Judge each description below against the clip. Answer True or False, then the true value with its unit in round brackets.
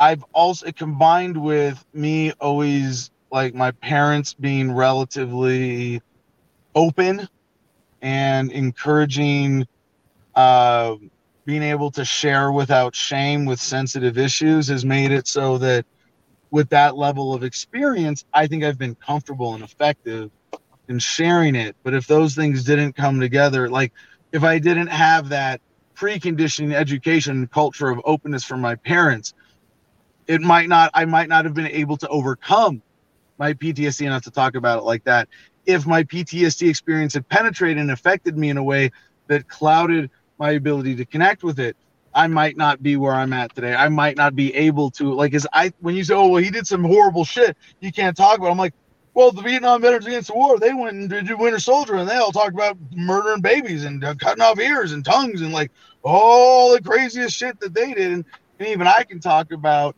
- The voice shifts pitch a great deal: False (4.4 semitones)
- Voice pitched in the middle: True (150 Hz)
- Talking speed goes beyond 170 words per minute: True (180 wpm)